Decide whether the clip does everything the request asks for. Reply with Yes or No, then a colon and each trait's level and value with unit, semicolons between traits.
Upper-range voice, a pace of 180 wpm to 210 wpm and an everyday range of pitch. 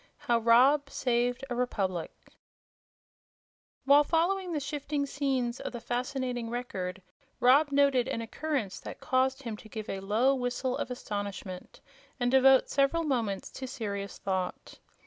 No: very high, 250 Hz; average, 140 wpm; average, 3.7 semitones